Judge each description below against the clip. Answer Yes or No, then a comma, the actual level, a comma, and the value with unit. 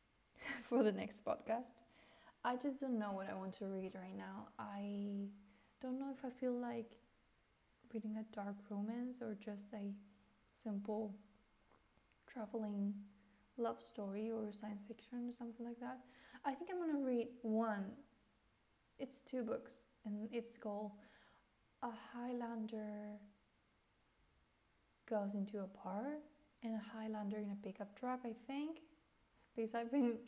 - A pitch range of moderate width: Yes, average, 3.2 semitones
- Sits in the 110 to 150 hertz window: No, high, 220 Hz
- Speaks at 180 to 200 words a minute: No, average, 140 wpm